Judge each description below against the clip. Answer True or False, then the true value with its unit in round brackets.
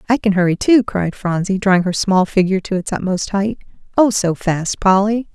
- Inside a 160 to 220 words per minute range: True (200 wpm)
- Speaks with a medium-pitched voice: False (195 Hz)